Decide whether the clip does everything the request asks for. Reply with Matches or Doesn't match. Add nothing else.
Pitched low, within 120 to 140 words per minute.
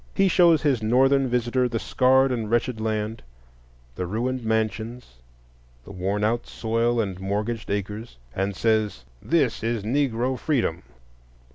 Matches